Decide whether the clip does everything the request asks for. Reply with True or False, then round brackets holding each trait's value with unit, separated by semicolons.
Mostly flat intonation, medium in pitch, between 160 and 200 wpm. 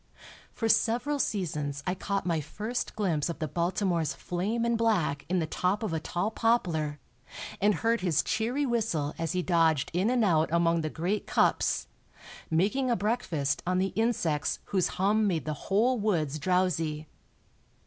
False (5.4 semitones; 180 Hz; 165 wpm)